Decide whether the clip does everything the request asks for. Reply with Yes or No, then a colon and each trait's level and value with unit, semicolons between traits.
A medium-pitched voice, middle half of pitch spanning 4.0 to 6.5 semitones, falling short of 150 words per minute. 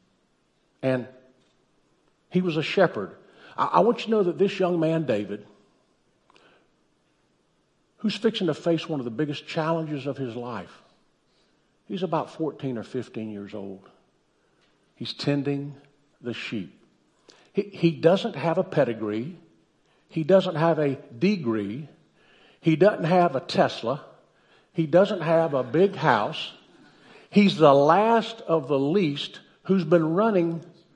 Yes: medium, 160 Hz; average, 5.2 semitones; slow, 135 wpm